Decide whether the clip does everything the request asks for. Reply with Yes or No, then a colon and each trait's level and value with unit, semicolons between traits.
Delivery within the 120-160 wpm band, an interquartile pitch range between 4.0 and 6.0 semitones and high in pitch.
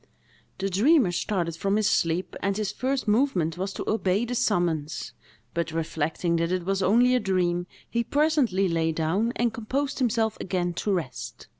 No: average, 170 wpm; average, 5.1 semitones; high, 195 Hz